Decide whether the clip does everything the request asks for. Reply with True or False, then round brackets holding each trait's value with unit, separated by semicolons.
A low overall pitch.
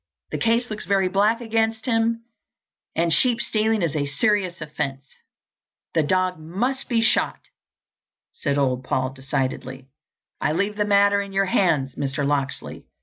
False (185 Hz)